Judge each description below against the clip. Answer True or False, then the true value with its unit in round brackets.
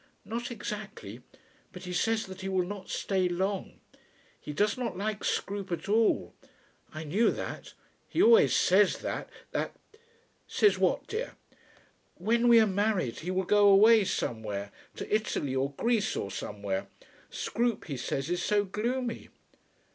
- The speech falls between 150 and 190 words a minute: True (155 wpm)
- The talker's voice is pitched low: False (200 Hz)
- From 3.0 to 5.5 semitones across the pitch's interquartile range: True (4.2 semitones)